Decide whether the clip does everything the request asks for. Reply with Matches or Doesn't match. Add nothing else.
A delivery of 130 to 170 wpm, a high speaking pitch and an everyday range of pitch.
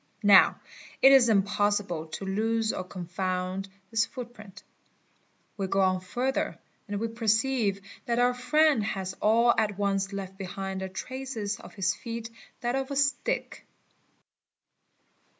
Matches